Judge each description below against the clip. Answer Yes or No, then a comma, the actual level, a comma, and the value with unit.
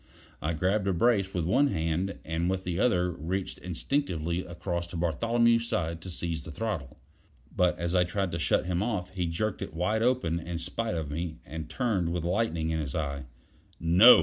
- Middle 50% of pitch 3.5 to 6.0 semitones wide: No, average, 3.1 semitones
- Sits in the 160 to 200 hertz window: No, very low, 90 Hz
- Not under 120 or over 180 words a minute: No, average, 195 wpm